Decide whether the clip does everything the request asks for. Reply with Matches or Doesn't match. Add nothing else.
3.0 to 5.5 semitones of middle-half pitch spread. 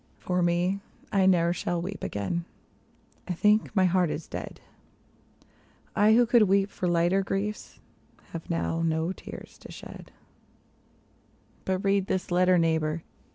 Doesn't match